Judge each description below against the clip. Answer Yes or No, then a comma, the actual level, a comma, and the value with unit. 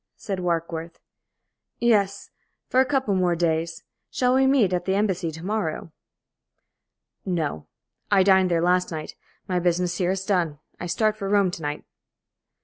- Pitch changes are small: No, average, 3.2 semitones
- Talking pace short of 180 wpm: Yes, average, 155 wpm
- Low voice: No, medium, 180 Hz